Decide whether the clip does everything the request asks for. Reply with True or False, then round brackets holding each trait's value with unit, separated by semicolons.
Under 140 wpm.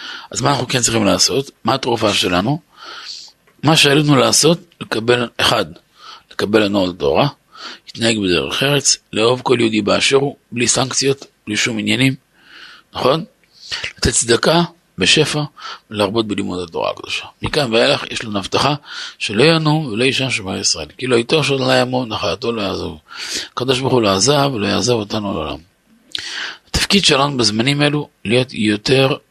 False (145 wpm)